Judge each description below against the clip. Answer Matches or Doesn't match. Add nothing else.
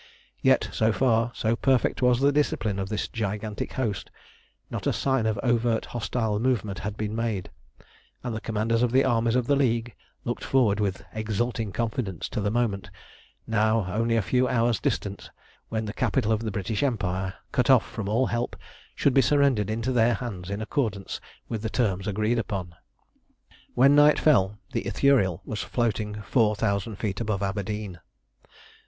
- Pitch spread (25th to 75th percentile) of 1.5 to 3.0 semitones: Matches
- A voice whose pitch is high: Doesn't match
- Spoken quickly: Doesn't match